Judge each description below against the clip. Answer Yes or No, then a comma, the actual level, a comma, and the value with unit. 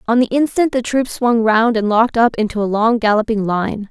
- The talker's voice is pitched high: Yes, high, 225 Hz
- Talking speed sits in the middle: No, fast, 230 wpm